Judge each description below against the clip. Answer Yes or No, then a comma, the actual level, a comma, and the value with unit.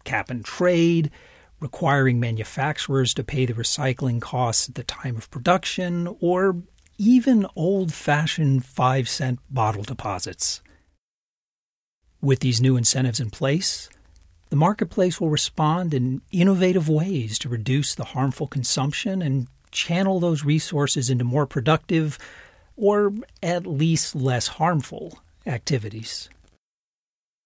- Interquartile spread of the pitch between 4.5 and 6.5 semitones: Yes, wide, 5.5 semitones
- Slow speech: Yes, slow, 120 wpm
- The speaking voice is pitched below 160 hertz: Yes, medium, 140 Hz